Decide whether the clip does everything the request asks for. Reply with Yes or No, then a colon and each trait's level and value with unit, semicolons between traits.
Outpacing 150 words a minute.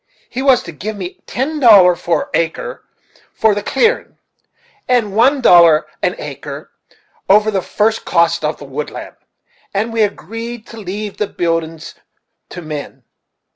No: average, 145 wpm